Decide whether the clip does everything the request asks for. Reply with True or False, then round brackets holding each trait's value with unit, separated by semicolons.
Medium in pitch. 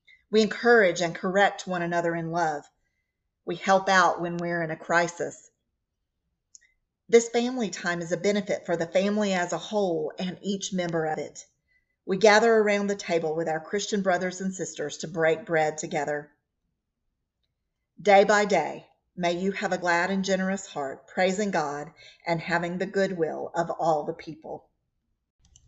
True (180 Hz)